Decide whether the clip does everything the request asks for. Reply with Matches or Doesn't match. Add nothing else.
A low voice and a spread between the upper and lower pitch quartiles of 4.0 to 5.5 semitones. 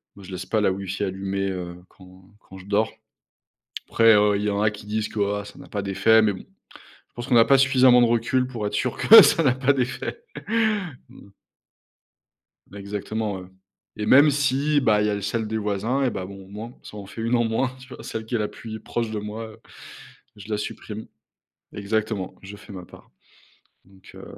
Doesn't match